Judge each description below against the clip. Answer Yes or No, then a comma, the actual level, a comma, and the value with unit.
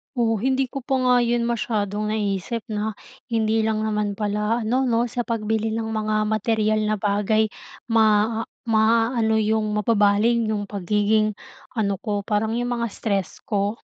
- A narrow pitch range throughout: Yes, narrow, 1.5 semitones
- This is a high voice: Yes, high, 220 Hz